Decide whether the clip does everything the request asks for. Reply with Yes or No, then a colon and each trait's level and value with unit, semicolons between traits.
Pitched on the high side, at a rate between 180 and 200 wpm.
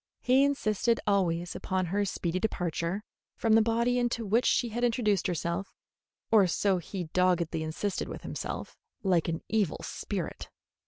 No: high, 200 Hz; average, 150 wpm